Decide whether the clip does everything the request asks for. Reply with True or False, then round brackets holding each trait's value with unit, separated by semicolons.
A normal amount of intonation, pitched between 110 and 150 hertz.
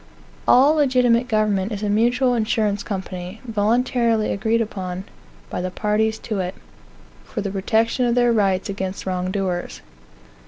False (3.4 semitones; 215 Hz)